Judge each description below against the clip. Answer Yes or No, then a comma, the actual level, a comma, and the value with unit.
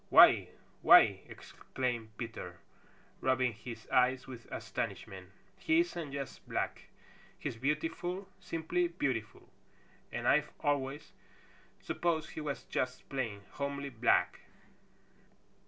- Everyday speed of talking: No, slow, 105 wpm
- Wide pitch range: No, average, 4.4 semitones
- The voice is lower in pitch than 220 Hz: Yes, low, 135 Hz